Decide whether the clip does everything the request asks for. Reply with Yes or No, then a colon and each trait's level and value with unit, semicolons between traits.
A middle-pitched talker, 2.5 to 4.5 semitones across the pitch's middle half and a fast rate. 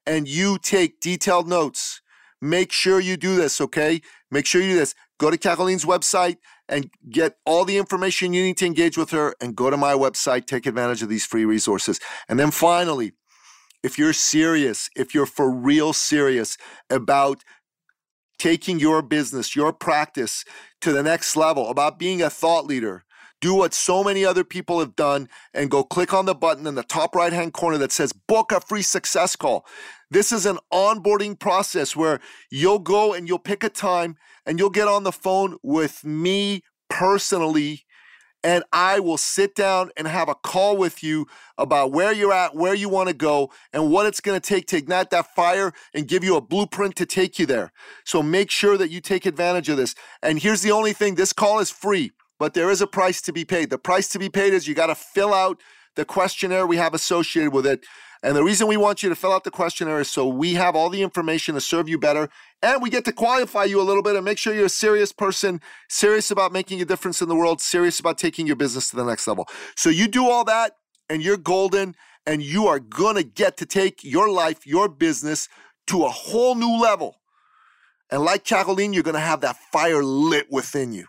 Yes: medium, 180 Hz; average, 4.0 semitones; fast, 215 wpm